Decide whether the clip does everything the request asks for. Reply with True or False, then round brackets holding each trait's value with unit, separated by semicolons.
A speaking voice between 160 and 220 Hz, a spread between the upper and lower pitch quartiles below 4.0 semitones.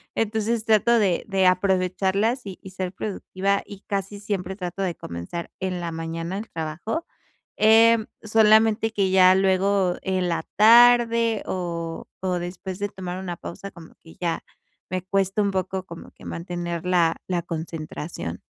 True (190 Hz; 3.1 semitones)